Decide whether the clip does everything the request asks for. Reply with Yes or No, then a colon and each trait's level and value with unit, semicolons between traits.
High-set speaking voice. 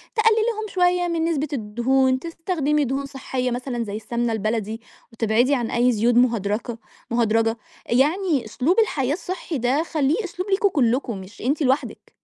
Yes: very high, 260 Hz